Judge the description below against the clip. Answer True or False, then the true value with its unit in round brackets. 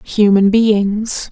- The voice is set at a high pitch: True (210 Hz)